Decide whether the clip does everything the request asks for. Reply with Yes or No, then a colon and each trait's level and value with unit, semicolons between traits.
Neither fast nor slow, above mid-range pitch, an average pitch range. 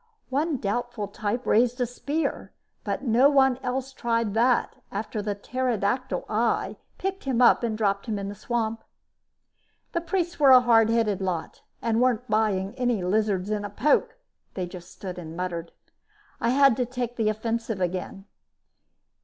Yes: average, 160 wpm; high, 230 Hz; average, 3.8 semitones